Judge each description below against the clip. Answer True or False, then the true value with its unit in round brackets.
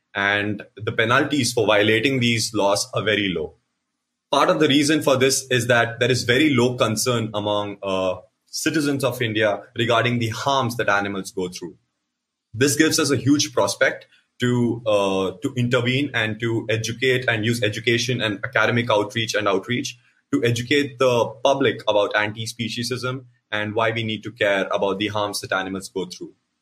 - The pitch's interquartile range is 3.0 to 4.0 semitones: True (3.4 semitones)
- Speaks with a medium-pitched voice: False (115 Hz)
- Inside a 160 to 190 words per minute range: True (170 wpm)